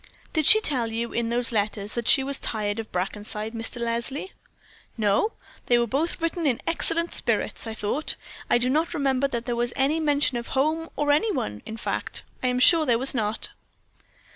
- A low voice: No, high, 245 Hz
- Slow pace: No, average, 195 wpm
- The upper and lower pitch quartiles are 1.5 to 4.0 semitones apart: No, average, 4.6 semitones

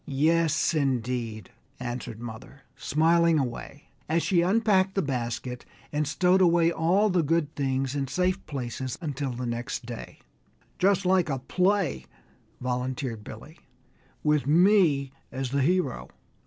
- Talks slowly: Yes, slow, 130 wpm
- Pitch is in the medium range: Yes, medium, 145 Hz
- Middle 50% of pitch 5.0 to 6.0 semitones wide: Yes, wide, 5.5 semitones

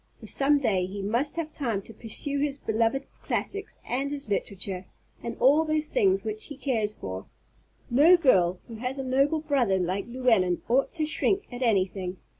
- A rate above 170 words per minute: Yes, average, 180 wpm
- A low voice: No, very high, 250 Hz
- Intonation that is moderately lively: No, wide, 6.4 semitones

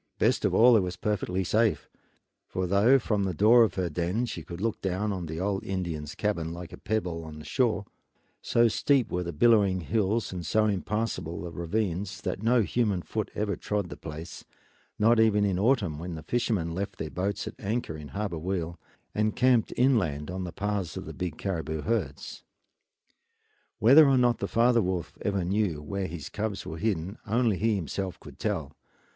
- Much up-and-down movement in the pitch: No, average, 4.2 semitones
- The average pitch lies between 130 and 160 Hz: No, low, 100 Hz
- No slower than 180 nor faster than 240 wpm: Yes, average, 190 wpm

